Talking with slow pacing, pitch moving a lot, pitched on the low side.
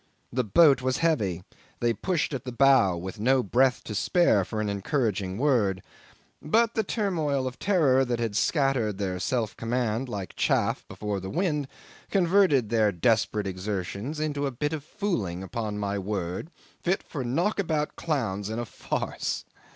No: average, 160 wpm; wide, 6.5 semitones; low, 120 Hz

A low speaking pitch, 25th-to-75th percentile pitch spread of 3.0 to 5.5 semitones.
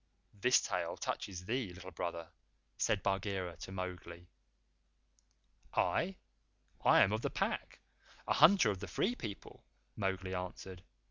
No: very low, 95 Hz; narrow, 2.6 semitones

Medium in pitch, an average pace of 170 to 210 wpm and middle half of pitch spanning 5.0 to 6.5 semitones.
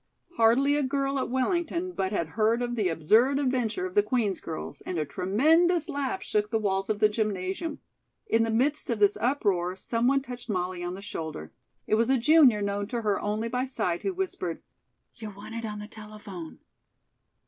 No: high, 225 Hz; average, 190 wpm; average, 5.3 semitones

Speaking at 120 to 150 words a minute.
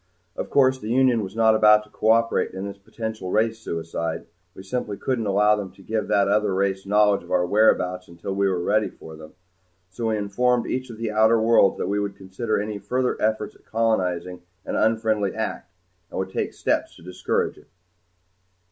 No: average, 195 wpm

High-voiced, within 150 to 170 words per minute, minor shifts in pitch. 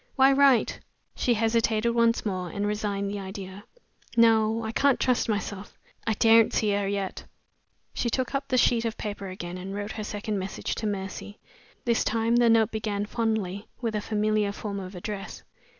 No: high, 215 Hz; average, 180 wpm; narrow, 2.3 semitones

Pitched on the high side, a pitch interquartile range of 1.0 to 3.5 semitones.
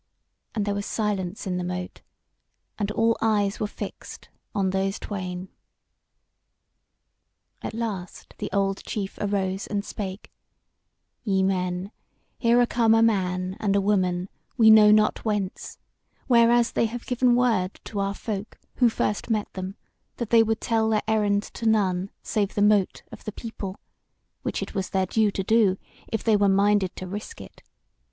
Yes: high, 205 Hz; narrow, 2.5 semitones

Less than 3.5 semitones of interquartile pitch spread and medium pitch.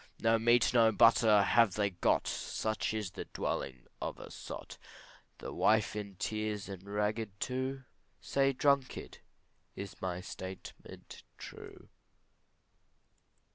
No: average, 2.8 semitones; low, 110 Hz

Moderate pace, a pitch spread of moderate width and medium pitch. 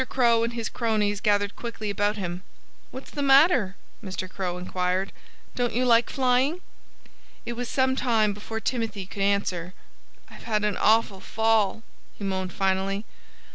No: average, 150 wpm; average, 3.5 semitones; high, 210 Hz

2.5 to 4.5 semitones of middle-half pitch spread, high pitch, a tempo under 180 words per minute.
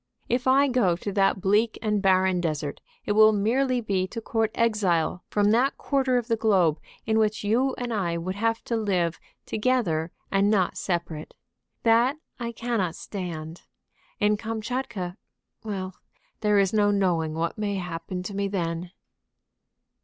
Yes: average, 3.9 semitones; high, 205 Hz; average, 155 wpm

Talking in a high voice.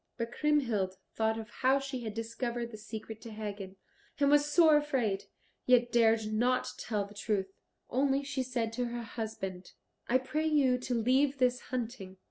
Yes: high, 240 Hz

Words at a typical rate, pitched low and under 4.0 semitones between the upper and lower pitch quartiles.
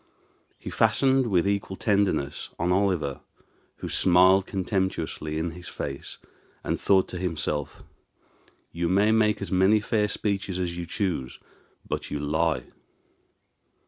No: slow, 130 wpm; very low, 95 Hz; average, 3.3 semitones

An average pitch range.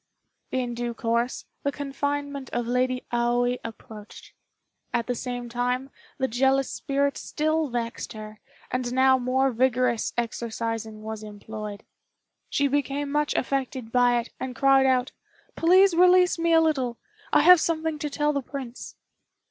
Yes: average, 3.0 semitones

